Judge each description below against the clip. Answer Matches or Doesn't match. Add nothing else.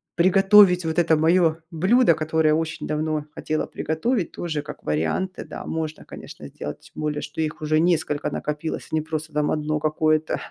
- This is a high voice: Doesn't match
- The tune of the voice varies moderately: Doesn't match